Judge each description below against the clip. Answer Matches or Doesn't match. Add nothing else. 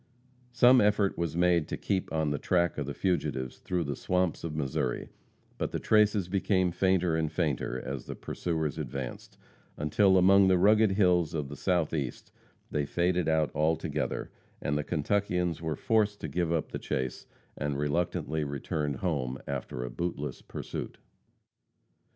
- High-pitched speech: Doesn't match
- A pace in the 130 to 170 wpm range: Matches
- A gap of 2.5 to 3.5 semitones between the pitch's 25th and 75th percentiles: Doesn't match